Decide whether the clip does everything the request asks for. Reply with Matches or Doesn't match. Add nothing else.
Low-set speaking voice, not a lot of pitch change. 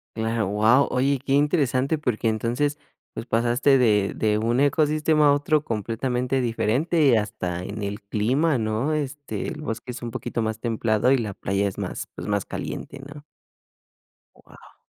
Doesn't match